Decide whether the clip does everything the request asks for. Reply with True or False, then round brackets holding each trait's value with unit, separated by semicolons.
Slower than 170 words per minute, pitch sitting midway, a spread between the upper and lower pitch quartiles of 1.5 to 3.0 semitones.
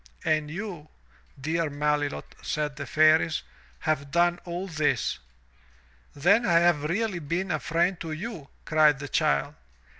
True (140 wpm; 155 Hz; 2.7 semitones)